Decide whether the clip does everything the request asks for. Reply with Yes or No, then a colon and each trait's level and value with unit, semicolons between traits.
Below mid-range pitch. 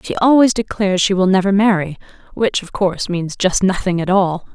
No: high, 190 Hz